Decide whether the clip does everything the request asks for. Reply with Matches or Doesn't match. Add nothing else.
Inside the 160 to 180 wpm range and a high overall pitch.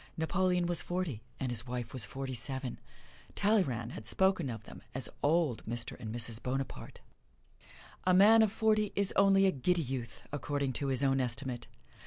Doesn't match